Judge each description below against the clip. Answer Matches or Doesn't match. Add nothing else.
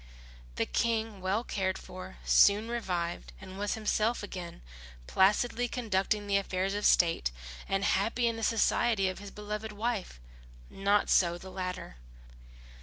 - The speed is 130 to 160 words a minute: Matches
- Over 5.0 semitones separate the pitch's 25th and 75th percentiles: Doesn't match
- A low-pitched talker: Doesn't match